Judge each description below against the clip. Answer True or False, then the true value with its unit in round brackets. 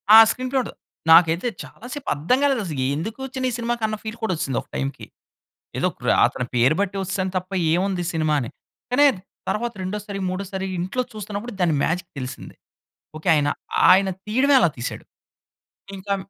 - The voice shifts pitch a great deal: True (5.9 semitones)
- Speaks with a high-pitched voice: True (195 Hz)